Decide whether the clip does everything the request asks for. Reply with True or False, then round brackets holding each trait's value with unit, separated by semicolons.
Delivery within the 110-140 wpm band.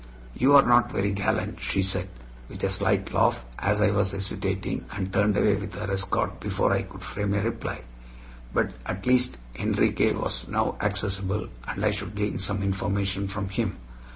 False (180 wpm)